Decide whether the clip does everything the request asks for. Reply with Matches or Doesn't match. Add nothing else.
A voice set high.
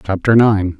Doesn't match